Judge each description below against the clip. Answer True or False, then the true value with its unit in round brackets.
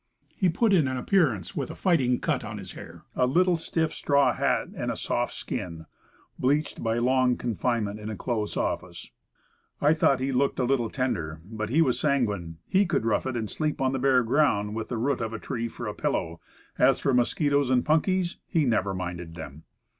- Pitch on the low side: True (125 Hz)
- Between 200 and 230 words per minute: True (205 wpm)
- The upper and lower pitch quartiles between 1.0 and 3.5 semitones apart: False (5.0 semitones)